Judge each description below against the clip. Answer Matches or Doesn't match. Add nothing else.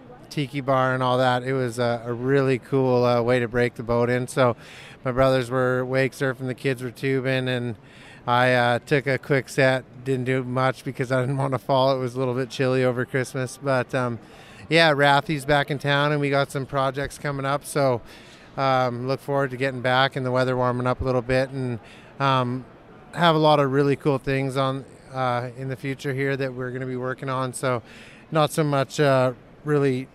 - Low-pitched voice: Matches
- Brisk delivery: Matches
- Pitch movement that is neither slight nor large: Doesn't match